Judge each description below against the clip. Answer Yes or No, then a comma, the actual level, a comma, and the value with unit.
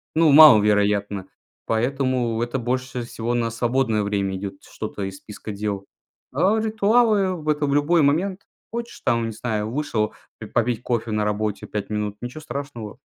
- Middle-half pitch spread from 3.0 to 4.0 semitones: No, wide, 5.6 semitones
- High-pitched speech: No, low, 120 Hz